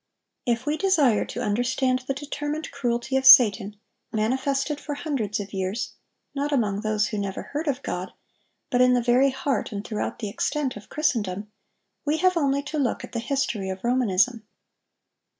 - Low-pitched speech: No, very high, 250 Hz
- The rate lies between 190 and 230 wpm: No, average, 170 wpm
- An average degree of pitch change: Yes, average, 5.0 semitones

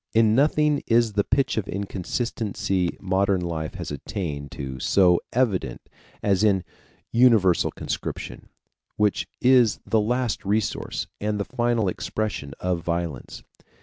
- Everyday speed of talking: No, slow, 125 wpm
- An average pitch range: Yes, average, 4.5 semitones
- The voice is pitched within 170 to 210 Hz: No, low, 100 Hz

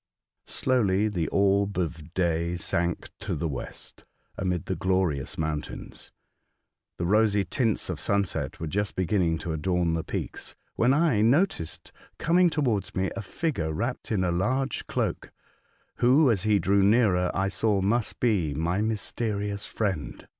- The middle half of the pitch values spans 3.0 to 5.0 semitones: Yes, average, 4.3 semitones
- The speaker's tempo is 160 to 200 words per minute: No, average, 145 wpm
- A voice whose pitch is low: Yes, low, 100 Hz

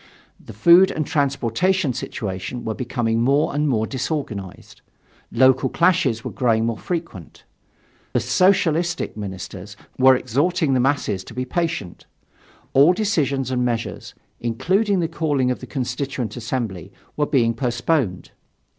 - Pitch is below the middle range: Yes, low, 130 Hz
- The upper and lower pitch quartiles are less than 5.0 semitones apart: No, wide, 5.6 semitones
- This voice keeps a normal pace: No, slow, 130 wpm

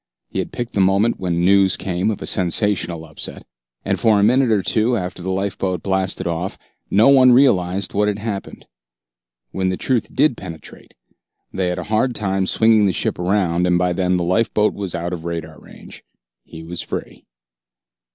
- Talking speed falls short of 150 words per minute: No, average, 185 wpm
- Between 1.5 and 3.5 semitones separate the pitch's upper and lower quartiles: Yes, average, 3.2 semitones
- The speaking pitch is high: No, very low, 95 Hz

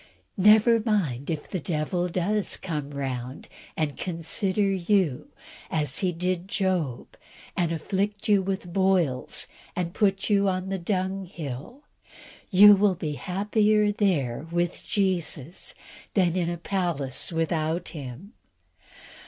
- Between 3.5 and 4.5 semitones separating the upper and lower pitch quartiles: Yes, average, 3.8 semitones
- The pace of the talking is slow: Yes, slow, 120 wpm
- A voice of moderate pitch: Yes, medium, 180 Hz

